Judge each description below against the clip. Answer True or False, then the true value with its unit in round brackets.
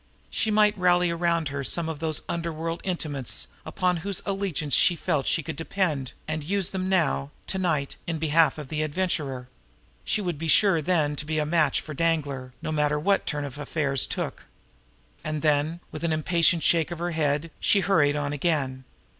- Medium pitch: True (160 Hz)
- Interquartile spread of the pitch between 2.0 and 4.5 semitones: True (3.0 semitones)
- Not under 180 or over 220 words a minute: True (185 wpm)